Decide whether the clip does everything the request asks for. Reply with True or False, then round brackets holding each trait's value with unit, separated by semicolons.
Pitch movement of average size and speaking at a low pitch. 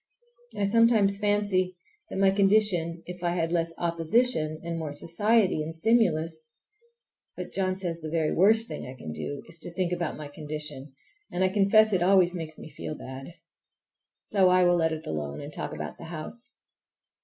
False (4.0 semitones; 175 Hz)